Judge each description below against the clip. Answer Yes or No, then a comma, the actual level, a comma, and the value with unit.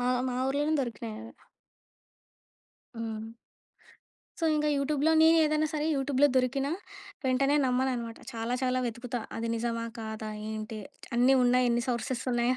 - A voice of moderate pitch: No, very high, 250 Hz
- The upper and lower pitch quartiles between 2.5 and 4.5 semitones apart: Yes, average, 2.9 semitones